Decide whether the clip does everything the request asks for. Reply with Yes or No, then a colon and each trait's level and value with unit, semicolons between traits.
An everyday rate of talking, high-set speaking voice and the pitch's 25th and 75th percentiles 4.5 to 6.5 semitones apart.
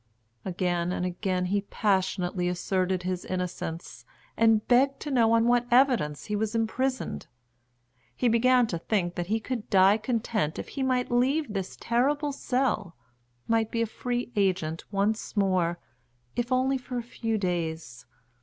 Yes: average, 155 wpm; high, 215 Hz; average, 5.1 semitones